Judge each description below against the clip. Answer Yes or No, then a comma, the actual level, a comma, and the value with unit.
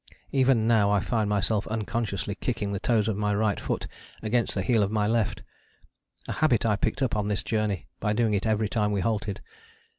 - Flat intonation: Yes, narrow, 1.9 semitones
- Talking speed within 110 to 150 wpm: No, fast, 205 wpm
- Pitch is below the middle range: Yes, low, 105 Hz